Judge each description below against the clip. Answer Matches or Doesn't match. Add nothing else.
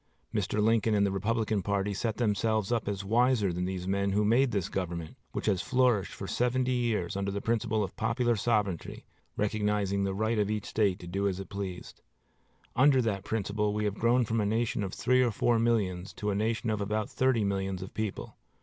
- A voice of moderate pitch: Doesn't match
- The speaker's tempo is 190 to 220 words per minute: Matches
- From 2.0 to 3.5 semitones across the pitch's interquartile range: Matches